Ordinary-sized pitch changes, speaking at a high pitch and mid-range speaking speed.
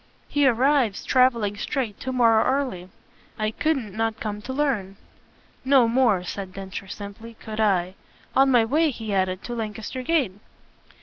Yes: average, 4.4 semitones; high, 225 Hz; average, 150 wpm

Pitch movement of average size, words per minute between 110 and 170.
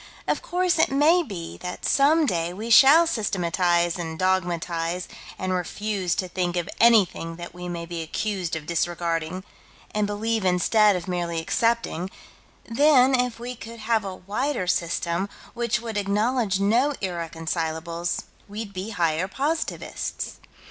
Yes: average, 5.0 semitones; average, 140 wpm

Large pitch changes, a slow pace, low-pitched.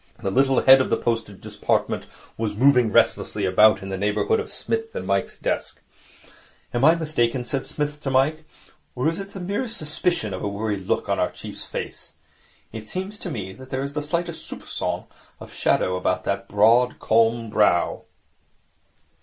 No: wide, 6.6 semitones; average, 180 wpm; low, 125 Hz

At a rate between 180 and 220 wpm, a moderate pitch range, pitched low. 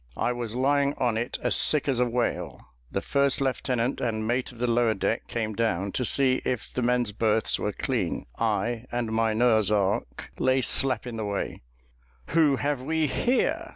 Yes: average, 190 wpm; average, 3.1 semitones; low, 120 Hz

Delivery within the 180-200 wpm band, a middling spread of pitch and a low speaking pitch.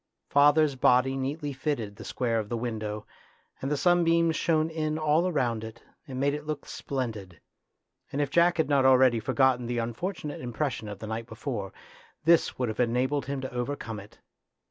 Yes: average, 190 wpm; average, 4.4 semitones; low, 130 Hz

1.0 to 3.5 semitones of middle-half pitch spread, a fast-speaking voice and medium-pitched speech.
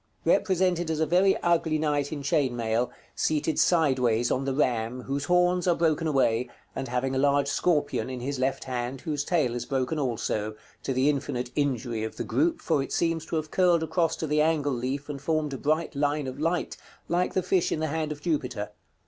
No: average, 3.9 semitones; fast, 210 wpm; medium, 145 Hz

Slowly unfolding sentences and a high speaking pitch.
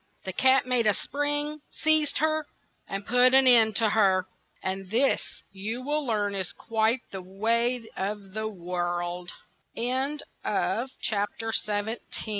Yes: slow, 120 wpm; high, 220 Hz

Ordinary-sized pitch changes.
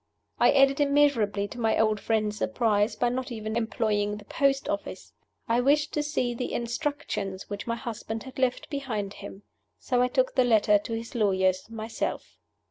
Yes: average, 3.7 semitones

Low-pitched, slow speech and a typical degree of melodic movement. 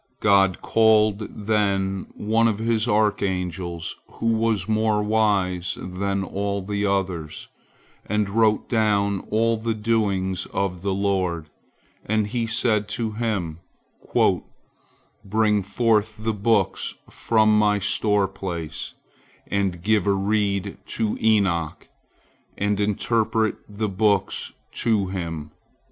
No: low, 105 Hz; slow, 115 wpm; narrow, 2.2 semitones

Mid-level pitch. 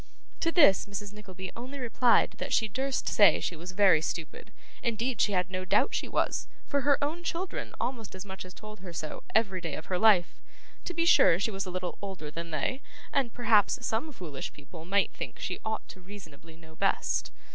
No: high, 200 Hz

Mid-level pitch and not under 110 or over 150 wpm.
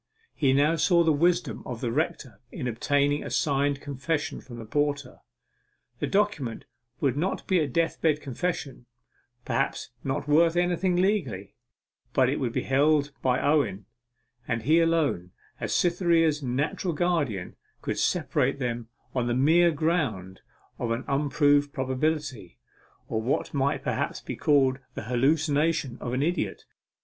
Yes: medium, 145 Hz; average, 145 wpm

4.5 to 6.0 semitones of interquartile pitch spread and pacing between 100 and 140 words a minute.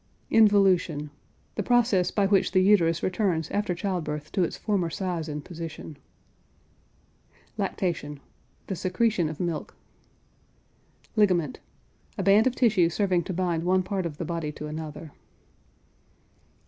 No: average, 3.5 semitones; slow, 135 wpm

